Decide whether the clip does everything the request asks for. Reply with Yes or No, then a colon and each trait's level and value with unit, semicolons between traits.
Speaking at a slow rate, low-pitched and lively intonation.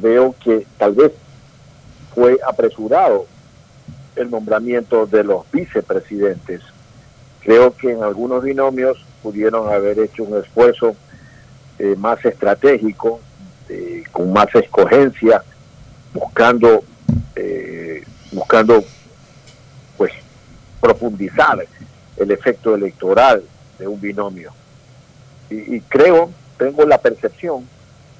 Yes: slow, 95 wpm; low, 130 Hz; wide, 6.9 semitones